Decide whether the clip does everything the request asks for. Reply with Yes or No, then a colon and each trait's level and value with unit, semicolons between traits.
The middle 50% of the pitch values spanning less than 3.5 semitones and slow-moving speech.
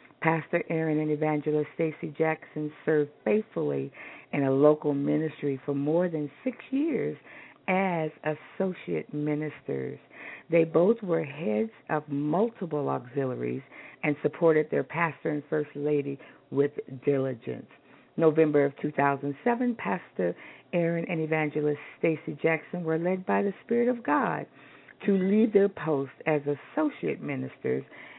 Yes: average, 2.7 semitones; slow, 125 wpm